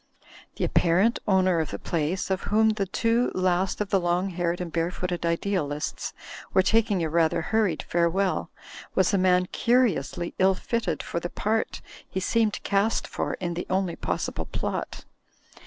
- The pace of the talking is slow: No, average, 170 wpm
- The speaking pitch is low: No, medium, 185 Hz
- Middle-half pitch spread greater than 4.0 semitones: No, average, 2.9 semitones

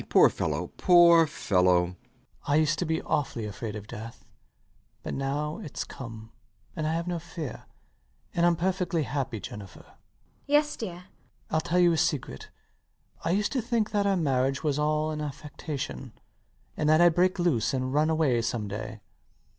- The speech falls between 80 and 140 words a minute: No, average, 180 wpm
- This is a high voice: No, medium, 155 Hz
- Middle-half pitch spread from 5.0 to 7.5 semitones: Yes, wide, 5.4 semitones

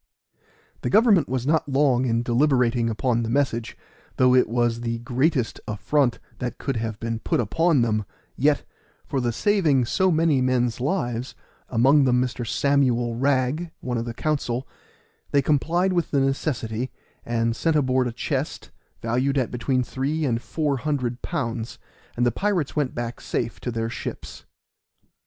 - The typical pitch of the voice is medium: No, low, 125 Hz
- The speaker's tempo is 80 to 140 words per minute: No, average, 160 wpm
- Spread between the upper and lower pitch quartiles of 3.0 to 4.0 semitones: Yes, average, 3.4 semitones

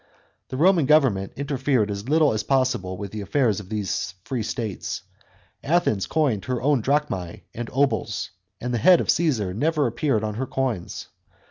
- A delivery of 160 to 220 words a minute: Yes, average, 165 wpm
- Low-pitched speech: Yes, low, 125 Hz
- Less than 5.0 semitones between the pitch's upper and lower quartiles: No, wide, 5.4 semitones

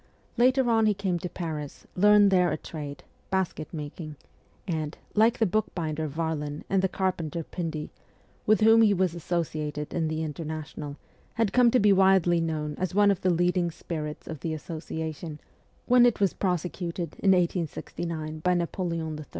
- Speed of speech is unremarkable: Yes, average, 165 wpm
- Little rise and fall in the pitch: No, average, 3.5 semitones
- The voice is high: No, medium, 170 Hz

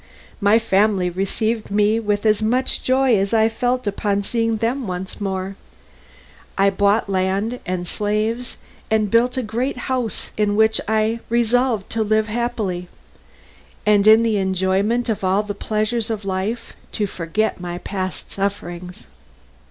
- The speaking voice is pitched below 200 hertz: No, high, 215 Hz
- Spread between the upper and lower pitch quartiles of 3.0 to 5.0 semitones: No, narrow, 2.6 semitones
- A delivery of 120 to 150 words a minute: Yes, average, 145 wpm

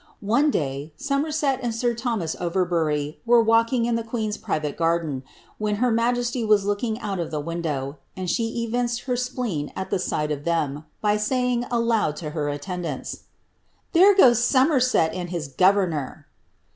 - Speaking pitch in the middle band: No, high, 210 Hz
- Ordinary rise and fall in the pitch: No, wide, 6.8 semitones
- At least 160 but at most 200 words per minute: Yes, average, 165 wpm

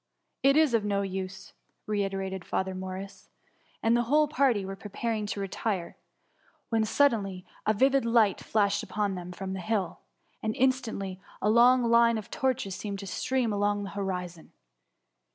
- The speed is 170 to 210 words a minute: No, average, 160 wpm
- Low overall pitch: No, high, 205 Hz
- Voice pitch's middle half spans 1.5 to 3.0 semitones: No, average, 3.4 semitones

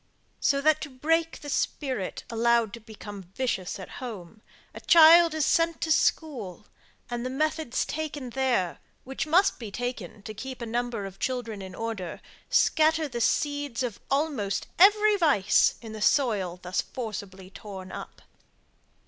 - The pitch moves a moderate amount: No, wide, 6.7 semitones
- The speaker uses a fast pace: No, average, 155 wpm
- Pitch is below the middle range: No, high, 245 Hz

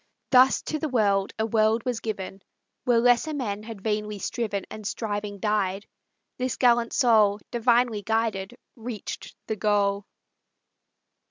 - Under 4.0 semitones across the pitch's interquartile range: Yes, average, 2.7 semitones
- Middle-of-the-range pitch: No, high, 220 Hz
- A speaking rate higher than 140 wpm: No, slow, 135 wpm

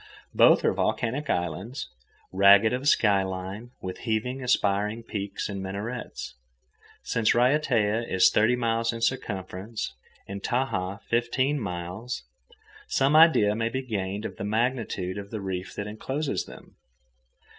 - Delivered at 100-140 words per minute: Yes, slow, 135 wpm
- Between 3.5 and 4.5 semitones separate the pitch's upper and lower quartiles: Yes, average, 3.9 semitones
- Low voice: Yes, low, 110 Hz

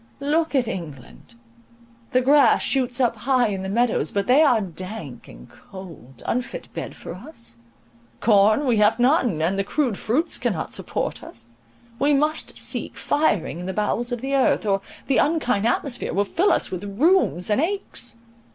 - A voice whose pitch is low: No, high, 230 Hz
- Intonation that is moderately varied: No, wide, 5.9 semitones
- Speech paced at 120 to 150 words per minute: No, average, 170 wpm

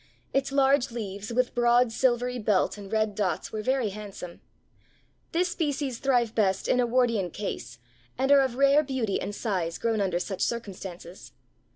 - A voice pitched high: Yes, high, 230 Hz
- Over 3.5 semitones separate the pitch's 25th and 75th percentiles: Yes, average, 4.5 semitones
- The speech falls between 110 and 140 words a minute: No, average, 165 wpm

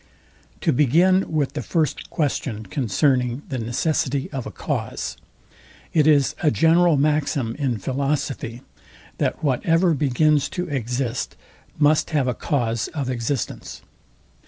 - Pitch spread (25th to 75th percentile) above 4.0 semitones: No, average, 3.6 semitones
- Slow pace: Yes, slow, 125 wpm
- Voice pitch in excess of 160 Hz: No, medium, 140 Hz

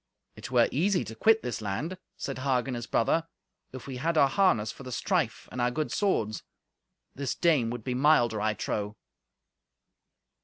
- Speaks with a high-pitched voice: No, low, 130 Hz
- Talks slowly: No, average, 170 wpm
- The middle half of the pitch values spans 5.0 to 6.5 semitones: Yes, wide, 5.5 semitones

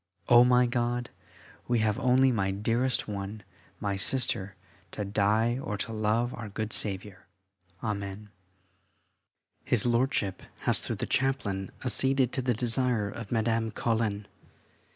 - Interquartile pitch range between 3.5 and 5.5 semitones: No, average, 3.1 semitones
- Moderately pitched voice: No, low, 115 Hz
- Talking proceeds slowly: Yes, slow, 130 wpm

